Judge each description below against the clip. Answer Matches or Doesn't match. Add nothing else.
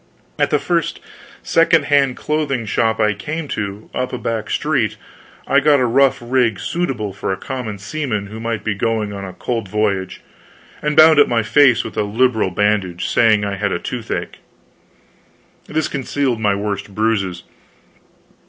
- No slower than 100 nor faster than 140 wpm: Doesn't match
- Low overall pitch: Matches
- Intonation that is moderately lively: Matches